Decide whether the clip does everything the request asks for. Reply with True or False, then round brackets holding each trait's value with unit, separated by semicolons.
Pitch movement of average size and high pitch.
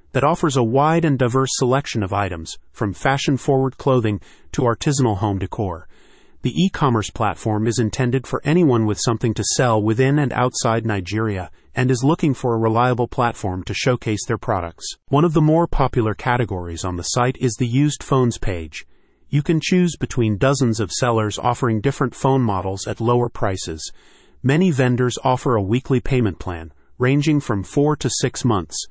False (3.8 semitones; 120 Hz)